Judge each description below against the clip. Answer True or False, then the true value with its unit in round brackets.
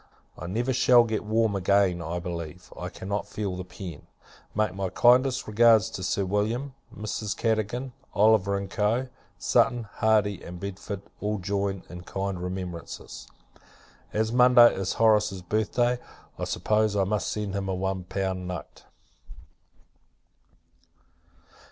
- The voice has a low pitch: True (100 Hz)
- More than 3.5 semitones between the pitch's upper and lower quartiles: False (2.8 semitones)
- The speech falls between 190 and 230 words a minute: False (135 wpm)